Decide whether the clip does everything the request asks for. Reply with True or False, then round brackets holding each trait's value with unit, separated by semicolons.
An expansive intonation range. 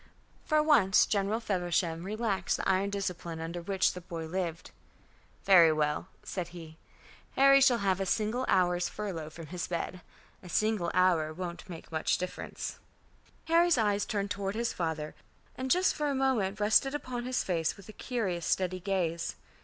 False (4.2 semitones)